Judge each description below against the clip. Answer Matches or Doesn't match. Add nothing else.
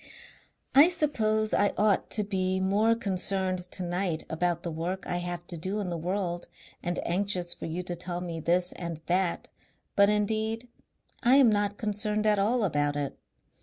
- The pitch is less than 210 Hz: Matches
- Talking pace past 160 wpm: Matches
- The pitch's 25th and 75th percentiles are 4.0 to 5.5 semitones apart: Doesn't match